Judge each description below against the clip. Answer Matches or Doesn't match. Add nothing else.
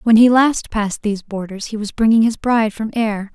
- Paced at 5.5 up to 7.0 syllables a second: Matches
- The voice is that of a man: Doesn't match